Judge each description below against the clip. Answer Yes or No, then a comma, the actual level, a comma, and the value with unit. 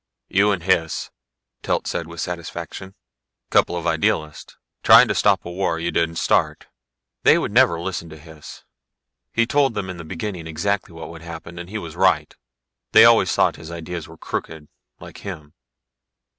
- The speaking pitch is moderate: No, very low, 85 Hz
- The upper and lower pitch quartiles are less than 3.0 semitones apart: Yes, narrow, 2.4 semitones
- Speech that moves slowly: No, average, 170 wpm